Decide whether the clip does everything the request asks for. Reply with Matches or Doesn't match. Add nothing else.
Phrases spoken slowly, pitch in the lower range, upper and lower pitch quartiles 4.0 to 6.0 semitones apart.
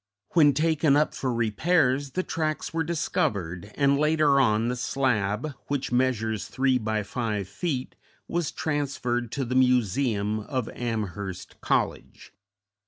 Matches